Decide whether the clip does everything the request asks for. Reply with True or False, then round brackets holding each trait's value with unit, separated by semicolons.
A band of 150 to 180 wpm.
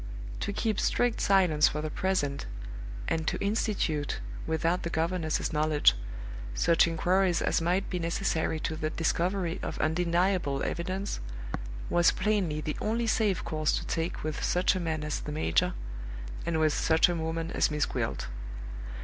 True (155 wpm)